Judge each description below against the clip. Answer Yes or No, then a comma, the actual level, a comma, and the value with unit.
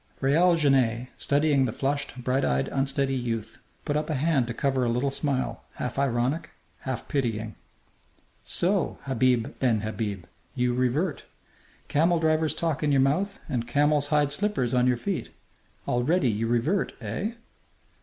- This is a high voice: No, low, 135 Hz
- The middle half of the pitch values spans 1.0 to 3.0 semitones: No, average, 3.8 semitones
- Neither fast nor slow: Yes, average, 150 wpm